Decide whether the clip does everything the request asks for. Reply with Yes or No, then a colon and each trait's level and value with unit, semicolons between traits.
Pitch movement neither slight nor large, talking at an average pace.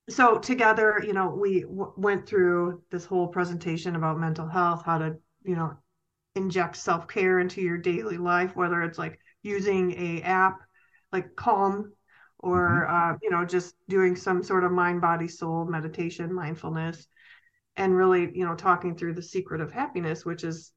No: narrow, 1.9 semitones; average, 170 wpm